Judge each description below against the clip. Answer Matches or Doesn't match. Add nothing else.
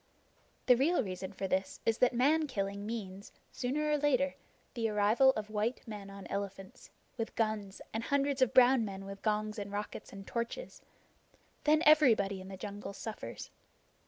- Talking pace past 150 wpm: Matches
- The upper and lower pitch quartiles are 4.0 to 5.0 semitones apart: Matches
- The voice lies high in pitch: Matches